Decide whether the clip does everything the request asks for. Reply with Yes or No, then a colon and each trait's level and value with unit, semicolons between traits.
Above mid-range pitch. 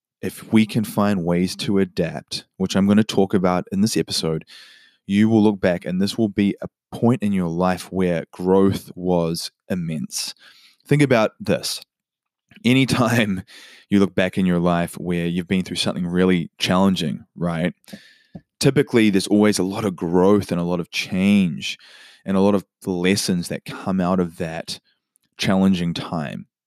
No: very low, 95 Hz